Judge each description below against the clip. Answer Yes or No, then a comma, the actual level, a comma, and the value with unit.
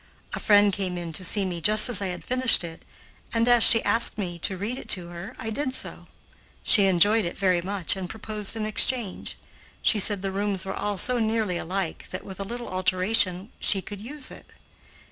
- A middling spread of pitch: Yes, average, 3.2 semitones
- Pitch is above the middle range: Yes, high, 200 Hz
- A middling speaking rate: No, fast, 210 wpm